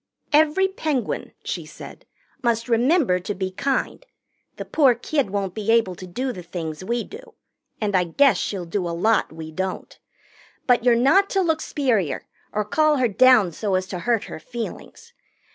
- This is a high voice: Yes, high, 230 Hz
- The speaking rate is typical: Yes, average, 180 wpm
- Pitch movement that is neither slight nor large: No, wide, 6.7 semitones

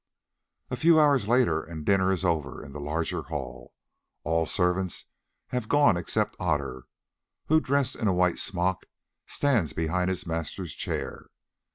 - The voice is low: Yes, very low, 90 Hz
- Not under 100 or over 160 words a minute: Yes, average, 155 wpm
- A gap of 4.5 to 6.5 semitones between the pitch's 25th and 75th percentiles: Yes, wide, 5.4 semitones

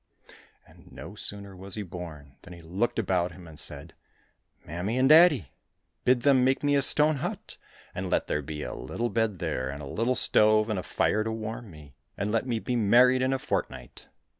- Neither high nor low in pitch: No, low, 110 Hz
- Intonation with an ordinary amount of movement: No, wide, 6.5 semitones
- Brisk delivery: Yes, fast, 210 wpm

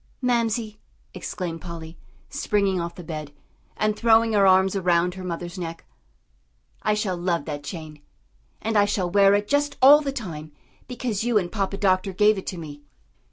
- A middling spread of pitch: Yes, average, 3.9 semitones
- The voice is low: No, high, 190 Hz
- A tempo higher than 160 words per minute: Yes, average, 170 wpm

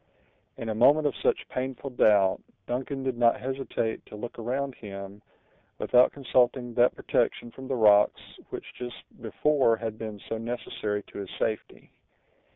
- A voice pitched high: No, low, 120 Hz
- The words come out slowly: No, average, 155 wpm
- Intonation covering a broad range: No, average, 3.3 semitones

